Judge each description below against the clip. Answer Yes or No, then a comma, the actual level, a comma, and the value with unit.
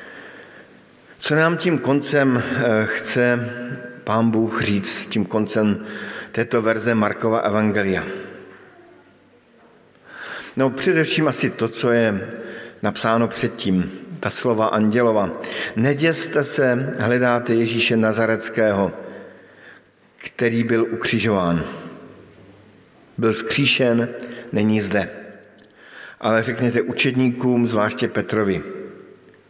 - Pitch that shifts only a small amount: Yes, narrow, 2.3 semitones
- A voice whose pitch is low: Yes, low, 115 Hz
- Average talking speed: No, slow, 85 wpm